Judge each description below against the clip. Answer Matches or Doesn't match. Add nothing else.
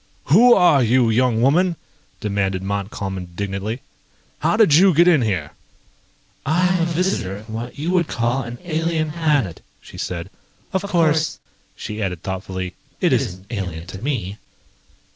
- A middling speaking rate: Matches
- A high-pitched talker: Doesn't match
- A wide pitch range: Matches